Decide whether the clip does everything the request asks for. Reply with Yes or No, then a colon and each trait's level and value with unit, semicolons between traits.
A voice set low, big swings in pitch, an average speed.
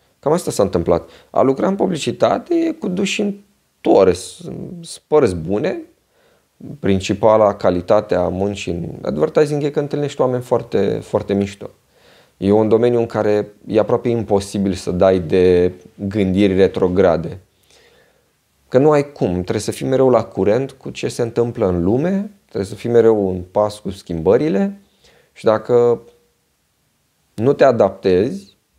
Yes: low, 110 Hz; wide, 6.7 semitones; average, 145 wpm